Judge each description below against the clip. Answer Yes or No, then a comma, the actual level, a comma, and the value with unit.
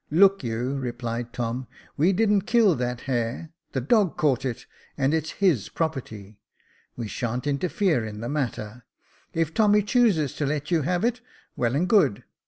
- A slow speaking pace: No, average, 185 wpm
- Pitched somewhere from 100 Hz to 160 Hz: Yes, medium, 140 Hz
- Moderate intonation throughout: No, wide, 7.1 semitones